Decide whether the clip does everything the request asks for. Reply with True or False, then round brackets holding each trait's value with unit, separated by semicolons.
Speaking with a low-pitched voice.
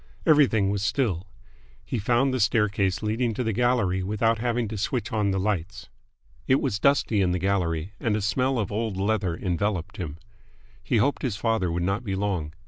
True (105 Hz)